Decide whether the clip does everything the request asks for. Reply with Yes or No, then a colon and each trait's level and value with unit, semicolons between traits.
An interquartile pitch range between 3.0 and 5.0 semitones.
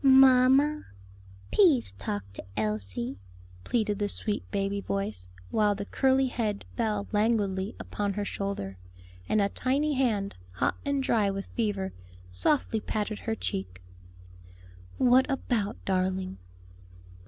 Yes: average, 4.4 semitones